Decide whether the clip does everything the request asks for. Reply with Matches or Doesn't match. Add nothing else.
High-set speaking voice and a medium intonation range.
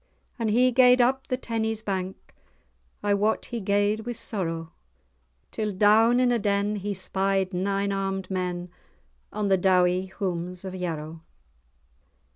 Matches